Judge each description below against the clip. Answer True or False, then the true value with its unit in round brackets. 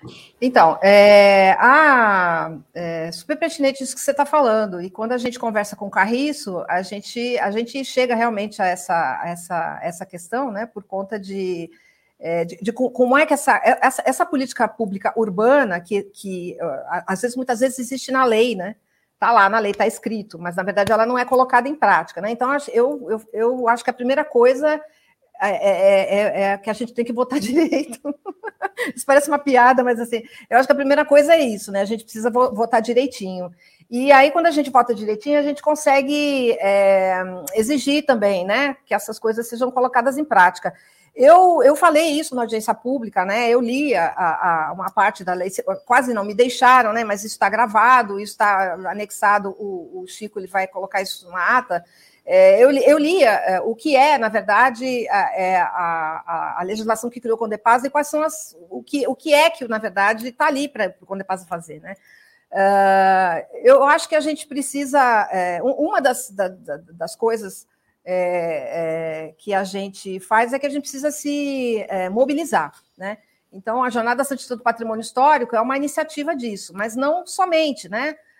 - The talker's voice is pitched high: True (235 Hz)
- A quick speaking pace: True (195 wpm)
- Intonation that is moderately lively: False (5.9 semitones)